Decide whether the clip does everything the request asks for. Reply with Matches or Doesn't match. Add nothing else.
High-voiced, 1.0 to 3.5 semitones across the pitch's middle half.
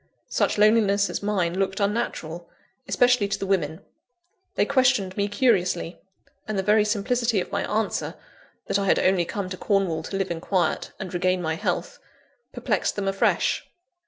Matches